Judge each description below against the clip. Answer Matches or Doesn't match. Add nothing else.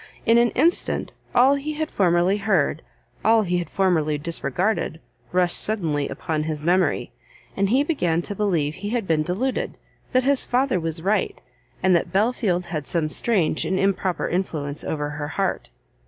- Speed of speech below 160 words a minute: Doesn't match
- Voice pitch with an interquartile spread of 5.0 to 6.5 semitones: Matches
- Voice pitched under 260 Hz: Matches